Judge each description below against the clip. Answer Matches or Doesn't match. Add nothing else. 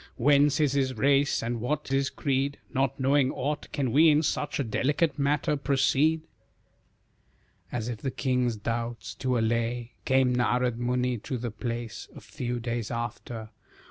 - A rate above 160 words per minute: Doesn't match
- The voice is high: Doesn't match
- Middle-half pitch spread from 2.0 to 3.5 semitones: Matches